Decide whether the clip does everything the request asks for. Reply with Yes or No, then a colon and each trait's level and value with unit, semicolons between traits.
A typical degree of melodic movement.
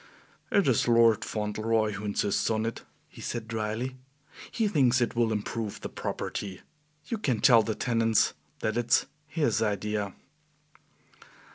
No: narrow, 2.2 semitones